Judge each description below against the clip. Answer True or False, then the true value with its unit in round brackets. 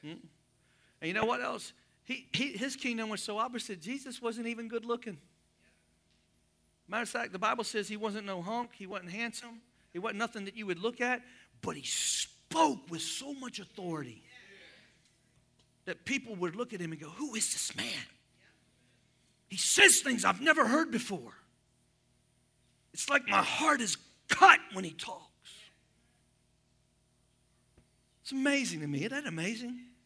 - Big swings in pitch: True (5.8 semitones)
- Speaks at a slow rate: False (160 wpm)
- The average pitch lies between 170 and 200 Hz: False (220 Hz)